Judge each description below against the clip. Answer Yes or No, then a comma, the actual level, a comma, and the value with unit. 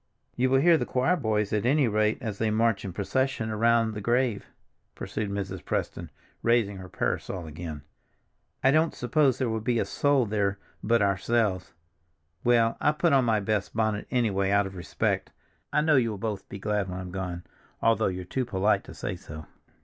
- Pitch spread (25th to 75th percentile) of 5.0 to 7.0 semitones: No, average, 3.8 semitones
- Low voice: Yes, low, 110 Hz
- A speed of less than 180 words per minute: No, average, 190 wpm